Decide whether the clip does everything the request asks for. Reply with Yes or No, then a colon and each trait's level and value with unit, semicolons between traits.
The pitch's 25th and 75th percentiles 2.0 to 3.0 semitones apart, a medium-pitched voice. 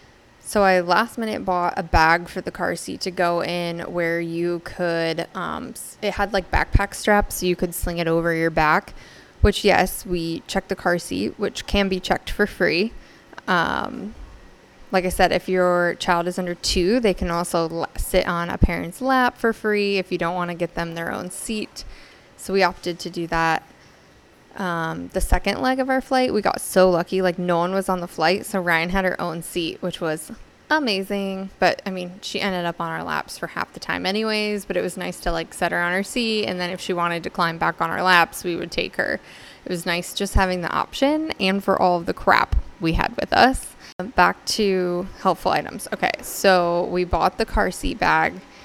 Yes: narrow, 2.4 semitones; medium, 180 Hz